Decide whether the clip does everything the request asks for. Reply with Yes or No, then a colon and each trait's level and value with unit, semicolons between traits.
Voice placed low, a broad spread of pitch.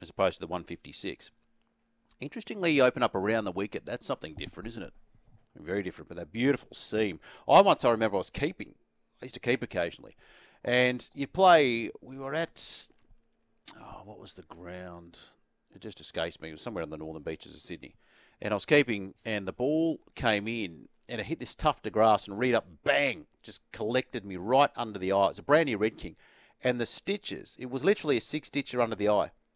Yes: low, 110 Hz; wide, 6.0 semitones